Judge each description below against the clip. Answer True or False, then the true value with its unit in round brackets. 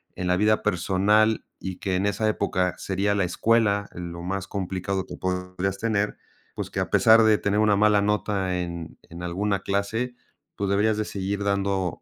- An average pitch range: False (2.2 semitones)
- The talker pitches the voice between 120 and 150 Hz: False (100 Hz)